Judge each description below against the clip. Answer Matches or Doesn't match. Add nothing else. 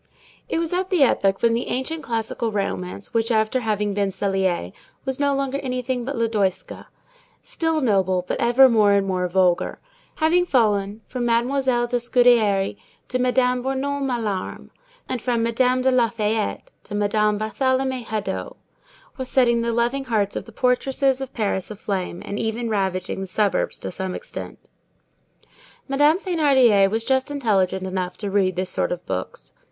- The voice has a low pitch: Doesn't match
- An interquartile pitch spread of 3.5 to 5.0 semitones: Matches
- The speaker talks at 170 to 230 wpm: Doesn't match